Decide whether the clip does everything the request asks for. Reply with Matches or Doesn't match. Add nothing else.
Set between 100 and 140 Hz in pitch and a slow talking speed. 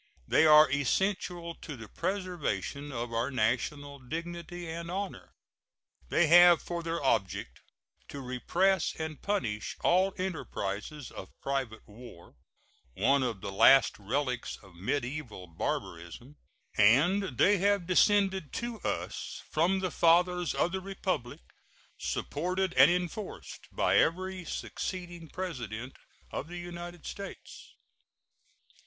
Doesn't match